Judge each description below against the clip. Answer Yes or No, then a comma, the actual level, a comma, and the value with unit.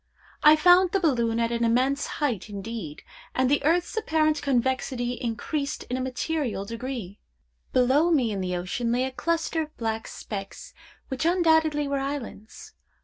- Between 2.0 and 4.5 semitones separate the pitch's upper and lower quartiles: No, average, 5.0 semitones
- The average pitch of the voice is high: Yes, very high, 260 Hz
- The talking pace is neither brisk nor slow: Yes, average, 155 wpm